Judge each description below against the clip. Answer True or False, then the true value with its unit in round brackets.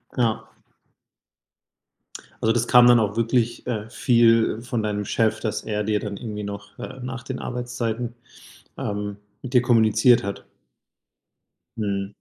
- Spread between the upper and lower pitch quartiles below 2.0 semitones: False (2.6 semitones)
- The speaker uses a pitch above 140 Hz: False (115 Hz)